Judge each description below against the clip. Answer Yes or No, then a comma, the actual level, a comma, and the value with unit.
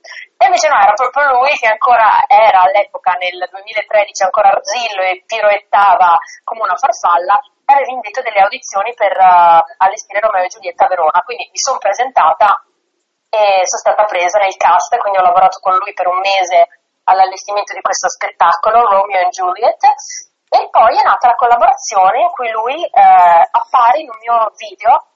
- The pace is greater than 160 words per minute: Yes, fast, 170 wpm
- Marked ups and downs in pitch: Yes, wide, 6.3 semitones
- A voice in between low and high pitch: No, high, 210 Hz